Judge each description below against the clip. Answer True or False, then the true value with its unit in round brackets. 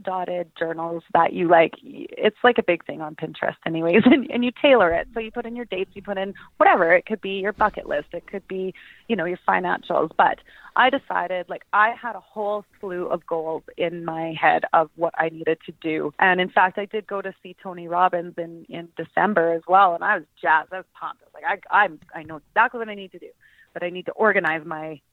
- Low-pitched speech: False (180 Hz)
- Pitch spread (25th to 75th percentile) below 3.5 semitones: False (4.1 semitones)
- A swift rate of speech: True (240 wpm)